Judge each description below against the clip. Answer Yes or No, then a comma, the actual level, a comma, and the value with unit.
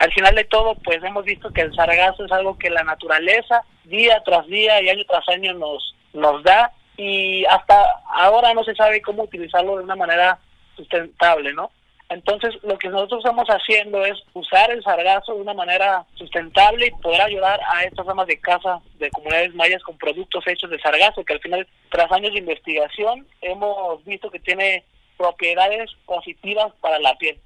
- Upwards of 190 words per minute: No, average, 185 wpm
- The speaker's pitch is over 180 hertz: Yes, high, 190 Hz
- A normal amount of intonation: Yes, average, 3.4 semitones